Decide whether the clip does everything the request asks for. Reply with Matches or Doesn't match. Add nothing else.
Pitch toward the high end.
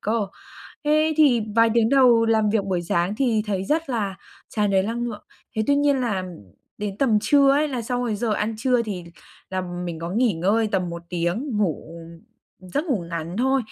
Matches